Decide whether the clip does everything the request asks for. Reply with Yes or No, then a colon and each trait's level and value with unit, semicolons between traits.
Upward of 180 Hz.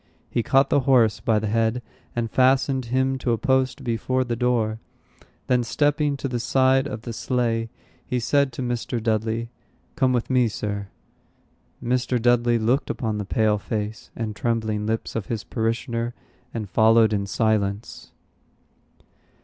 No: low, 115 Hz